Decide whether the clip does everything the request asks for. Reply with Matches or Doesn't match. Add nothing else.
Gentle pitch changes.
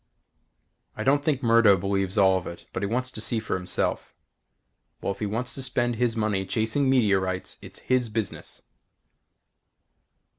Doesn't match